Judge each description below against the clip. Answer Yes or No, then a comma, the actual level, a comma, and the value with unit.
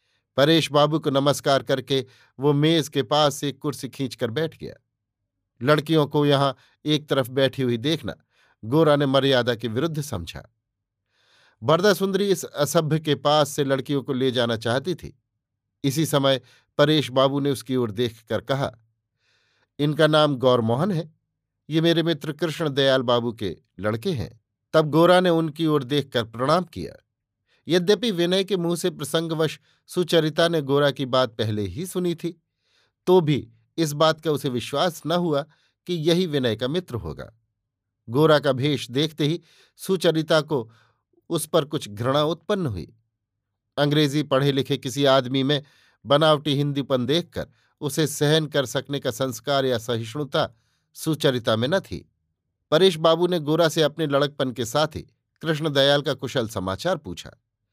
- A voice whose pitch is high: No, medium, 140 Hz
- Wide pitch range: No, average, 4.5 semitones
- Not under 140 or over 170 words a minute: Yes, average, 155 wpm